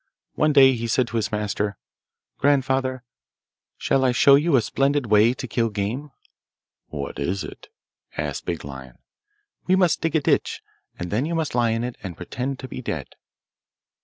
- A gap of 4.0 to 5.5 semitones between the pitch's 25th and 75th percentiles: Yes, average, 5.0 semitones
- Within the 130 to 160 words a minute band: No, average, 175 wpm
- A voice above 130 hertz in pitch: No, low, 125 Hz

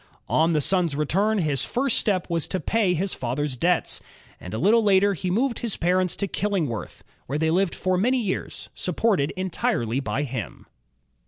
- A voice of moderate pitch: Yes, medium, 180 Hz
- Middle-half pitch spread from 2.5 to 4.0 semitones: No, average, 5.3 semitones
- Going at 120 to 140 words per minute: No, average, 175 wpm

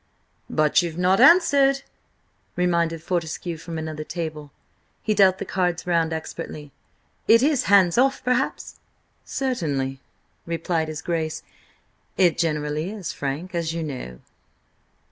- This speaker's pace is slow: Yes, slow, 125 wpm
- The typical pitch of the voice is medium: Yes, medium, 170 Hz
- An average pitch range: Yes, average, 3.4 semitones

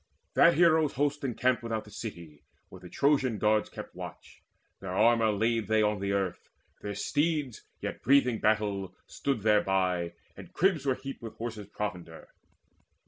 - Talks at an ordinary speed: Yes, average, 155 wpm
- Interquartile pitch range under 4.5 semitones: No, average, 5.0 semitones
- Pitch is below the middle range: Yes, low, 110 Hz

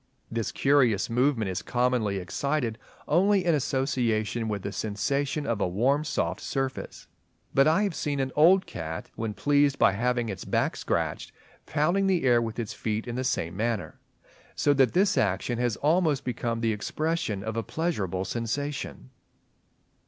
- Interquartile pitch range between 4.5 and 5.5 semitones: Yes, average, 4.9 semitones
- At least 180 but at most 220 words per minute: No, average, 160 wpm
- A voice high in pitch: No, low, 125 Hz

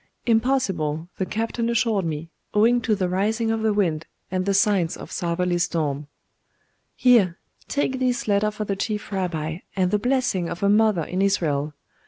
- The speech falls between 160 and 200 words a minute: Yes, average, 170 wpm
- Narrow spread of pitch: No, average, 4.5 semitones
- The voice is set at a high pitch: Yes, high, 200 Hz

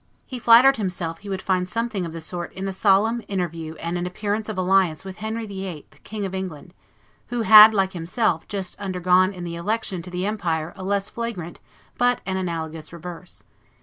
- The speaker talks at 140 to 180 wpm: No, average, 190 wpm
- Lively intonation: No, average, 3.4 semitones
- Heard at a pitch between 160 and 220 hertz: Yes, high, 190 Hz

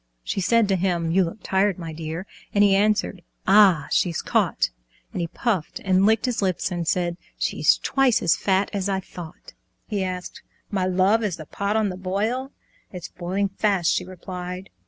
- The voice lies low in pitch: No, high, 190 Hz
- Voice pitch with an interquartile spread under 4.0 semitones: Yes, narrow, 2.4 semitones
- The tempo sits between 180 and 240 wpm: Yes, average, 185 wpm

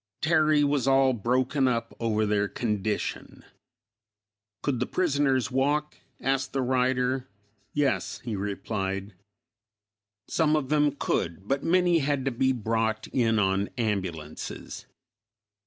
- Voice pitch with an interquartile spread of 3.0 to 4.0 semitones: No, average, 4.7 semitones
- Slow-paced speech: Yes, slow, 120 wpm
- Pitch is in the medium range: No, low, 130 Hz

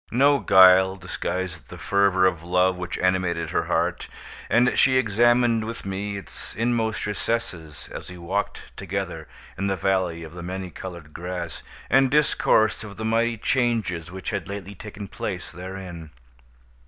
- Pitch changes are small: No, average, 3.7 semitones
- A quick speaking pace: No, average, 155 wpm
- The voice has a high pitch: No, very low, 95 Hz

